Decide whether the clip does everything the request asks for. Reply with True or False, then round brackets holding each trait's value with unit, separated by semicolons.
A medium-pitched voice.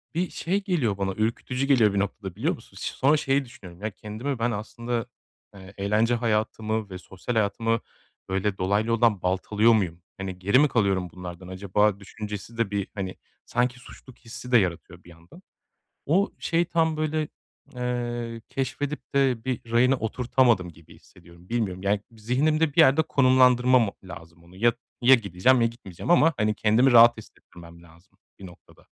False (115 Hz)